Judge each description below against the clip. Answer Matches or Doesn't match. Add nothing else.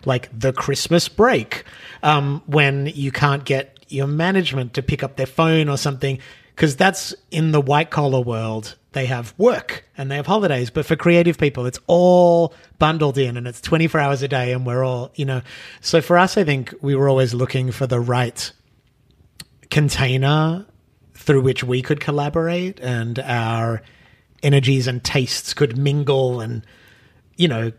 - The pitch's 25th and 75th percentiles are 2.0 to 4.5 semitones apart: Matches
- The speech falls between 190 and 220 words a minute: Doesn't match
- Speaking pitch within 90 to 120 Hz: Doesn't match